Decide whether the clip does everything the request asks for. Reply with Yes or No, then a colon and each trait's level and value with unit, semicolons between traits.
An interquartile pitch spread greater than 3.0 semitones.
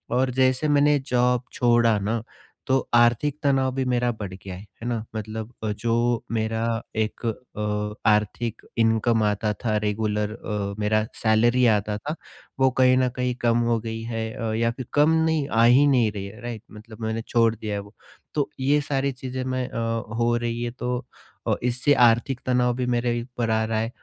No: narrow, 2.4 semitones